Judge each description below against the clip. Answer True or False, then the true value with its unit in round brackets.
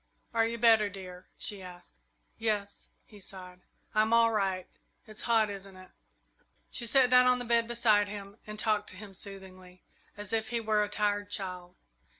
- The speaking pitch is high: True (210 Hz)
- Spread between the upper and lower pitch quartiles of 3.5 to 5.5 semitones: False (2.9 semitones)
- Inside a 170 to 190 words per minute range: True (175 wpm)